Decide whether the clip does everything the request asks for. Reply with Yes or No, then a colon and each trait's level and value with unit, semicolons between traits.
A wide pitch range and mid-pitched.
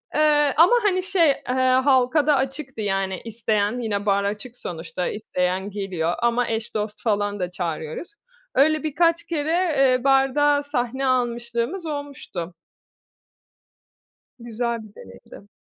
No: wide, 6.0 semitones; high, 240 Hz